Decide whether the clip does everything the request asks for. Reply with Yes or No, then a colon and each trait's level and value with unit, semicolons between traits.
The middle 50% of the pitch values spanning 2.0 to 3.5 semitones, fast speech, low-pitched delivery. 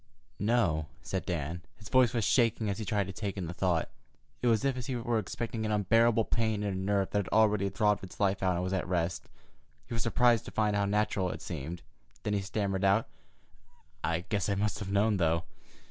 Yes: average, 2.9 semitones; fast, 225 wpm; low, 100 Hz